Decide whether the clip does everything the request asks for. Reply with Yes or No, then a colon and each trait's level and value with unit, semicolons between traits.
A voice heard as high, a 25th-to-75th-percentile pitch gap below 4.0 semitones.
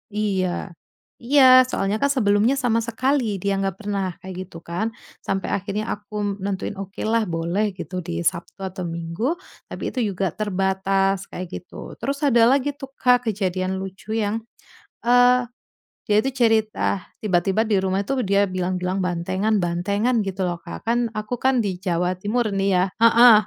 Yes: high, 200 Hz; average, 3.5 semitones